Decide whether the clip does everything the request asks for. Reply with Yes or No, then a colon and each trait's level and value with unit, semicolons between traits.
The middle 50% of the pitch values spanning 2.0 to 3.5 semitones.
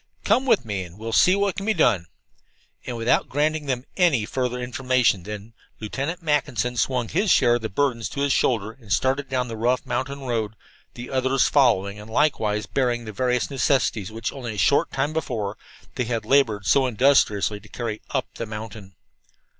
No: average, 4.1 semitones